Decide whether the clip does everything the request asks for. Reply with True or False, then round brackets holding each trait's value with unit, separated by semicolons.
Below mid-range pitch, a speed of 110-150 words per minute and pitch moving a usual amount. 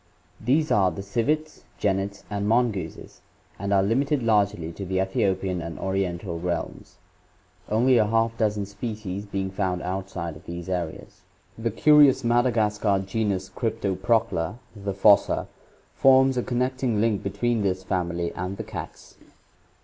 True (100 Hz; 140 wpm; 3.5 semitones)